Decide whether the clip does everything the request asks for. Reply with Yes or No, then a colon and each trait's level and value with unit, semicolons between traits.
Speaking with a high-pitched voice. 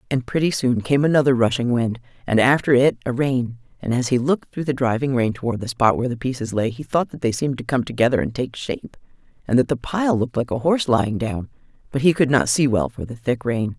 No: low, 125 Hz